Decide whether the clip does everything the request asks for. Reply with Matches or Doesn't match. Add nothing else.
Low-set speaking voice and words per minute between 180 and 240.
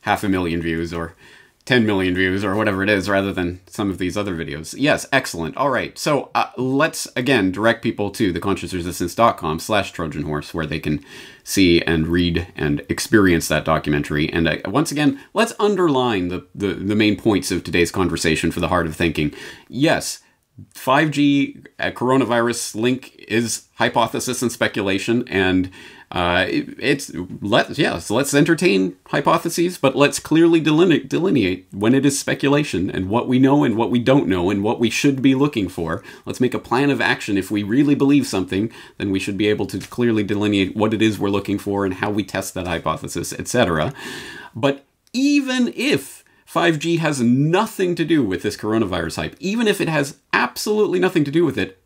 Matches